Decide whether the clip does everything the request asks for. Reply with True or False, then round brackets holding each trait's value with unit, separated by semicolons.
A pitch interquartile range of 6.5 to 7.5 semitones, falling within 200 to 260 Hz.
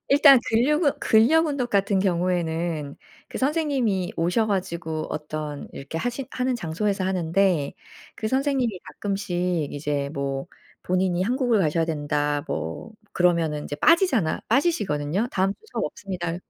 False (6.8 semitones; 185 Hz)